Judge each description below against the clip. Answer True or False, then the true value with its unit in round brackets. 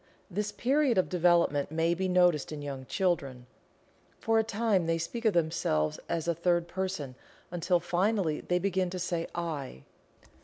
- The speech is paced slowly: False (160 wpm)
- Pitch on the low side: False (175 Hz)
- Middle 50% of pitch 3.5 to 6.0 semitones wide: False (3.0 semitones)